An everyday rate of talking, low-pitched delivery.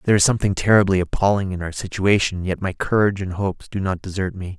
No: fast, 220 wpm; very low, 95 Hz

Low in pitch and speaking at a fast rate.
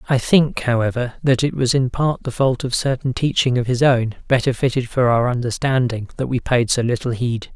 Yes: low, 125 Hz; fast, 215 wpm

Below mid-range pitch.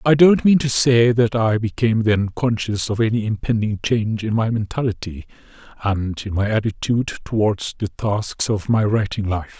Yes: low, 110 Hz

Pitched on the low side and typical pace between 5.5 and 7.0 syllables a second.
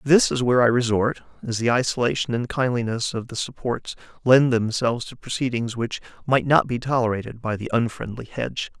Yes: low, 120 Hz; 5.6 syllables/s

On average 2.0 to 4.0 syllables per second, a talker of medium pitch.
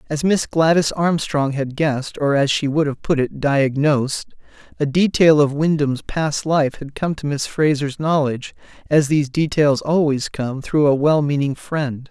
Yes: 3.9 syllables/s; medium, 145 Hz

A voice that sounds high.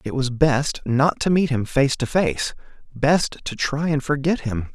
No: medium, 140 Hz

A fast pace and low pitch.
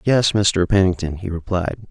No: average, 155 wpm; very low, 95 Hz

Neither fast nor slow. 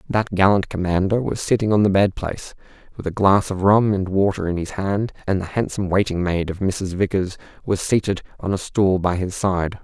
No: fast, 215 wpm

